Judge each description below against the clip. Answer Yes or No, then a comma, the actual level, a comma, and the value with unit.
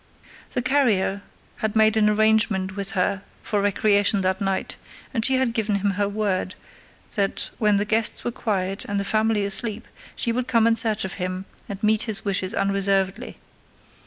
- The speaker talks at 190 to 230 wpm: No, average, 175 wpm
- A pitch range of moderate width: No, narrow, 2.0 semitones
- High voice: Yes, high, 205 Hz